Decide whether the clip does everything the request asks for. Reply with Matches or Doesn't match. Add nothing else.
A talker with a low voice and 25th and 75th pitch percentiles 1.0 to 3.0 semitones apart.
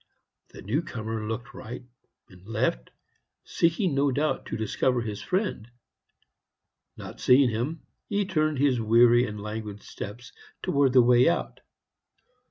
Doesn't match